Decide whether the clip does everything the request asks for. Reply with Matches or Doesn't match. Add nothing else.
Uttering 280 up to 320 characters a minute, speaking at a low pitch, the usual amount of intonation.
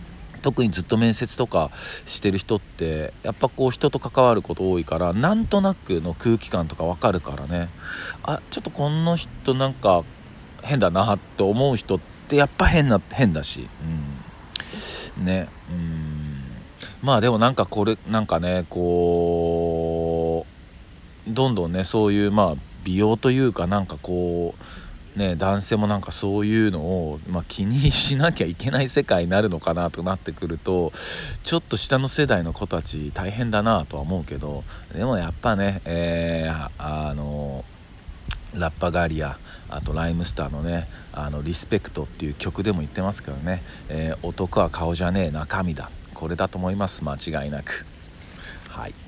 Matches